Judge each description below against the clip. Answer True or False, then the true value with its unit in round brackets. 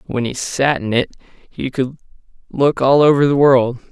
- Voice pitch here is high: False (135 Hz)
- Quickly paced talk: False (185 wpm)